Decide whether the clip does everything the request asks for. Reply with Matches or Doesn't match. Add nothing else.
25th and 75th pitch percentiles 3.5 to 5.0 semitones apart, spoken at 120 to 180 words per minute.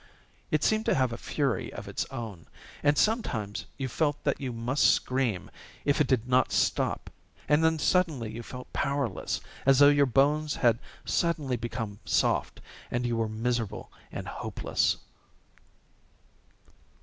Matches